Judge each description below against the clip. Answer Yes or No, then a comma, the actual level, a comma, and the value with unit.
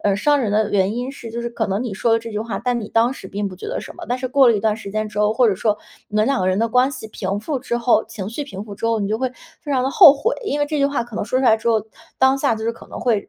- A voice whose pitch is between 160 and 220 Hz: No, high, 230 Hz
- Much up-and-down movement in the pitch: No, average, 3.4 semitones